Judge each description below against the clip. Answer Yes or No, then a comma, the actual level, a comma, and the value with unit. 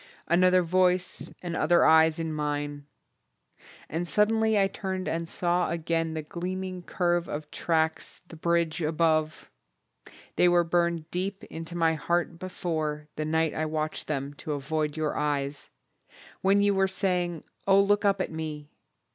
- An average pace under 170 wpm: Yes, average, 150 wpm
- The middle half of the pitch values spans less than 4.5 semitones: Yes, average, 2.7 semitones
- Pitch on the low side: No, medium, 165 Hz